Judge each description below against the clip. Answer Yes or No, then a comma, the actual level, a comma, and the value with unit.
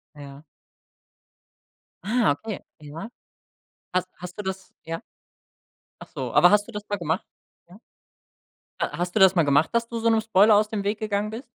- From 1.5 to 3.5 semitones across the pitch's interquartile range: No, average, 4.3 semitones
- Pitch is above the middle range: Yes, high, 200 Hz